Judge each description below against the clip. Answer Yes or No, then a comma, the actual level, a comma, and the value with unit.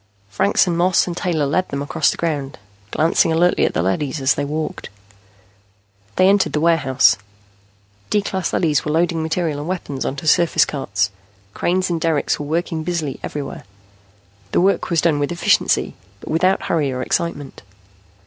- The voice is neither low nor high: Yes, medium, 160 Hz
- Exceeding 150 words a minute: Yes, average, 165 wpm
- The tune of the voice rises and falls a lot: No, average, 3.2 semitones